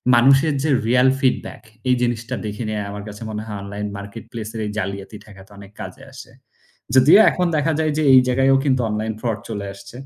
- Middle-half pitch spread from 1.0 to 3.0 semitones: No, average, 4.0 semitones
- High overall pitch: No, low, 115 Hz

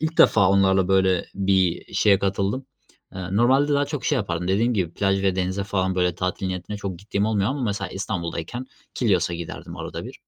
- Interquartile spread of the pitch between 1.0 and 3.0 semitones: Yes, narrow, 2.5 semitones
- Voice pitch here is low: Yes, very low, 95 Hz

